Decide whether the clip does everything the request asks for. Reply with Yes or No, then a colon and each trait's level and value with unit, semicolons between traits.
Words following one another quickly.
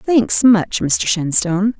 No: slow, 135 wpm